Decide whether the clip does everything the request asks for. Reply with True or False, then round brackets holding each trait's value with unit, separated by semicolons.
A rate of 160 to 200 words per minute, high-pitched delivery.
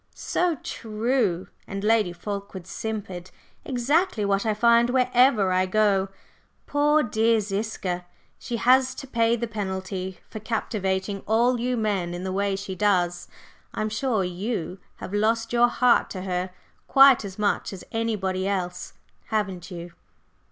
False (145 wpm; 210 Hz)